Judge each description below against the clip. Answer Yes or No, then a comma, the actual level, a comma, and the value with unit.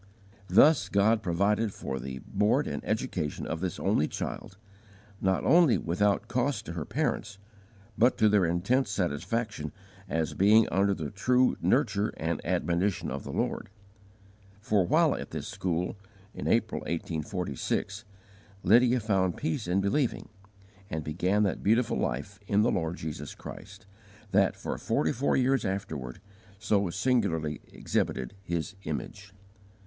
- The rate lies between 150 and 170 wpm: No, average, 140 wpm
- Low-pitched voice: Yes, low, 100 Hz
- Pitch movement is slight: No, average, 4.5 semitones